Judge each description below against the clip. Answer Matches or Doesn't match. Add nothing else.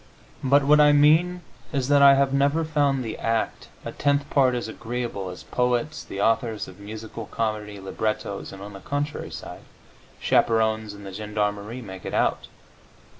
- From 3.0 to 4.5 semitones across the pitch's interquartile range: Doesn't match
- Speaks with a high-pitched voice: Doesn't match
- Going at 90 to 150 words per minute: Doesn't match